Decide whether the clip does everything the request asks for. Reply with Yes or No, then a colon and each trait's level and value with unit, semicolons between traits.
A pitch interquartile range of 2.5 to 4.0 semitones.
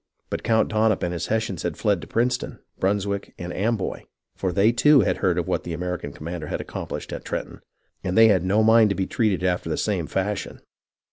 Yes: average, 3.7 semitones